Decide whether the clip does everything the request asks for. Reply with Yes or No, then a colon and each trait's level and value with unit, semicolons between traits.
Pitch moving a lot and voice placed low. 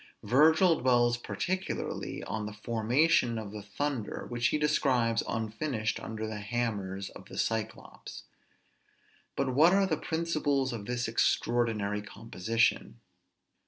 No: average, 4.8 semitones; low, 120 Hz